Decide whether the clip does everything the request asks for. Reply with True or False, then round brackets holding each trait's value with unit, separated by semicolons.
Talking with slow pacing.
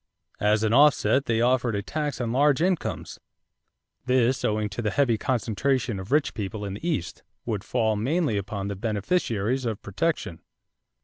False (165 wpm)